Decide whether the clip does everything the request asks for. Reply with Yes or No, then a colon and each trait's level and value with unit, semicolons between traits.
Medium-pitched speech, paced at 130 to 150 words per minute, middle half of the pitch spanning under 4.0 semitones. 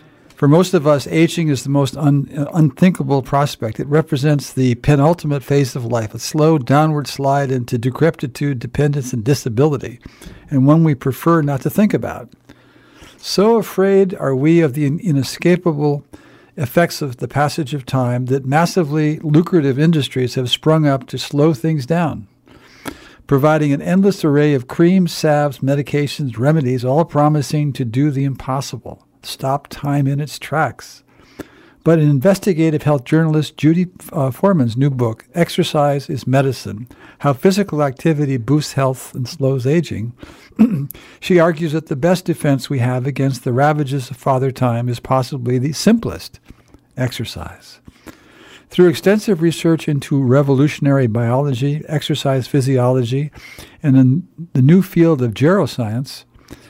Yes: medium, 145 Hz; average, 140 wpm; average, 3.3 semitones